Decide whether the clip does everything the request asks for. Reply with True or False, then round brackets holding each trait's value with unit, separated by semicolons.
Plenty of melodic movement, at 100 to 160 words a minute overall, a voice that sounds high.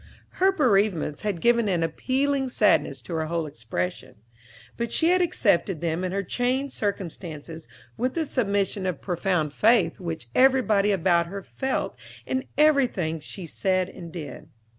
True (7.0 semitones; 150 wpm; 195 Hz)